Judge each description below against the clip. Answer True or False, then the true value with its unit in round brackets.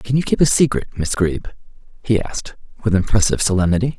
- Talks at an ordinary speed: True (180 wpm)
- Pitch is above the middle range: False (105 Hz)